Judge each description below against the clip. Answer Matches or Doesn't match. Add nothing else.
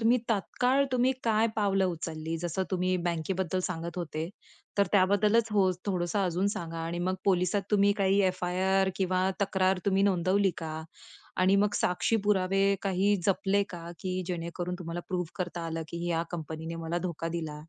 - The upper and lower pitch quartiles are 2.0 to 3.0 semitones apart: Matches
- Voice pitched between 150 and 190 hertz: Matches